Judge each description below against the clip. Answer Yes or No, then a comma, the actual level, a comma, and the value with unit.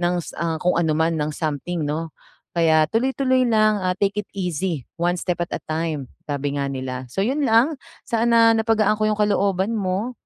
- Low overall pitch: No, medium, 180 Hz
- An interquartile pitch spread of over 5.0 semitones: Yes, wide, 5.6 semitones